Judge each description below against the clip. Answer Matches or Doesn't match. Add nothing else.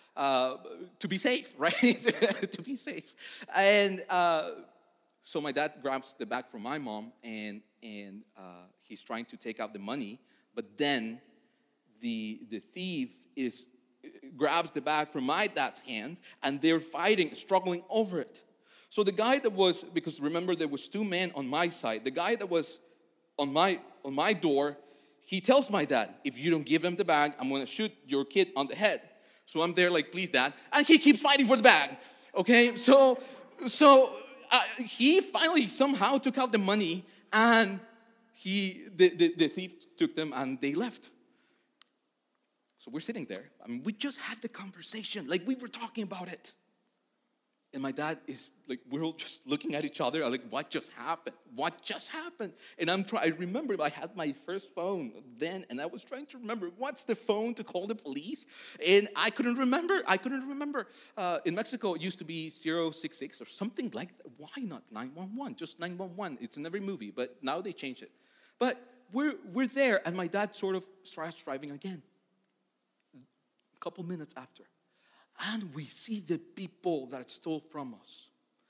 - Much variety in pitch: Matches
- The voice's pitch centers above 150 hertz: Matches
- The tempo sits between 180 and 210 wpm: Matches